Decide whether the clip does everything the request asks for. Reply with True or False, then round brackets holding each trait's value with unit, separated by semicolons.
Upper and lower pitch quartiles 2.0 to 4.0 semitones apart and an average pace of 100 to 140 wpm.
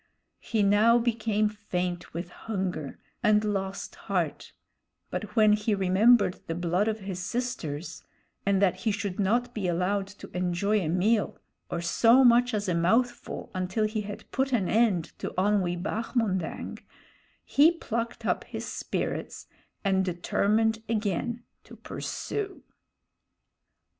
True (3.5 semitones; 135 wpm)